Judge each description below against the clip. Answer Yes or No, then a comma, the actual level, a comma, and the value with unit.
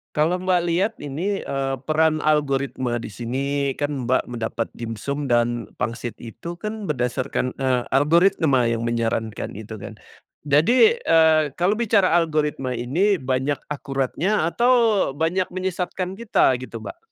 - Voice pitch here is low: No, medium, 145 Hz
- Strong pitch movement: Yes, wide, 5.9 semitones